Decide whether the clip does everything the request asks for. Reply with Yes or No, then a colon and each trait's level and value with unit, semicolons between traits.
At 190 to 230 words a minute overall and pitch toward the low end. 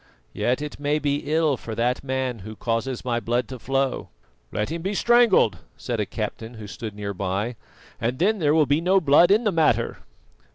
Yes: average, 200 wpm; low, 130 Hz